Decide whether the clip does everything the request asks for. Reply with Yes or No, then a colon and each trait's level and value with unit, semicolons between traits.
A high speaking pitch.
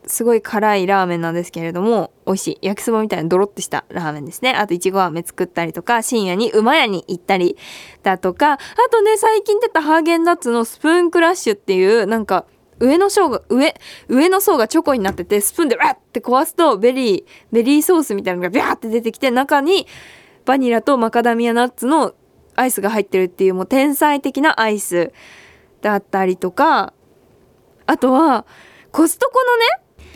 Yes: high, 235 Hz